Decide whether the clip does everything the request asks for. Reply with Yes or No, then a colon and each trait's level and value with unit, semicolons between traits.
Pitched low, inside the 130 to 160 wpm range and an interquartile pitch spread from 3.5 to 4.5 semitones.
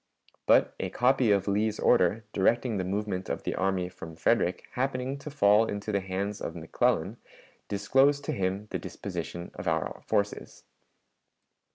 Yes: low, 100 Hz; average, 155 wpm; average, 4.0 semitones